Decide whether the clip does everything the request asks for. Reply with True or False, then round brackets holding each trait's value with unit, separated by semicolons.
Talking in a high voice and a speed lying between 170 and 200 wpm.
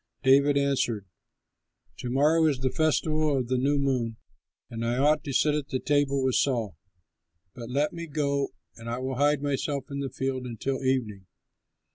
False (135 Hz; 175 wpm)